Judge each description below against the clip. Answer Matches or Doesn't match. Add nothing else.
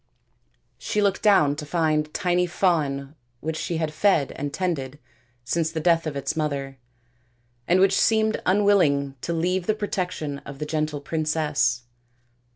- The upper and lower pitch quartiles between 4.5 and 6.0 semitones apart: Doesn't match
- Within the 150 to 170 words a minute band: Matches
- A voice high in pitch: Doesn't match